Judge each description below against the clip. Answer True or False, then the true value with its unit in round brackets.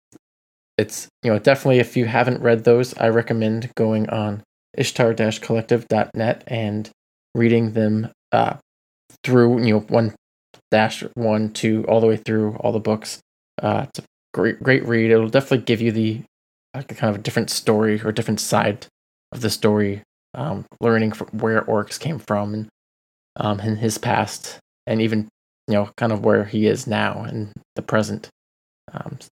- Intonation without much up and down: True (1.5 semitones)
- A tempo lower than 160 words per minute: False (165 wpm)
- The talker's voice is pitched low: True (110 Hz)